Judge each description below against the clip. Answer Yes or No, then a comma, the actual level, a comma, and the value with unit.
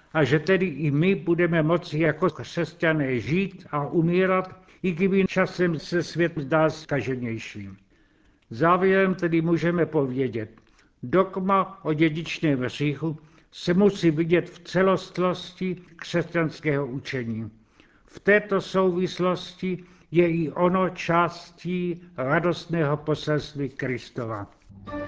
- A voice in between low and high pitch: Yes, medium, 165 Hz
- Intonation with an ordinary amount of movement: Yes, average, 3.7 semitones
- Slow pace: Yes, slow, 105 wpm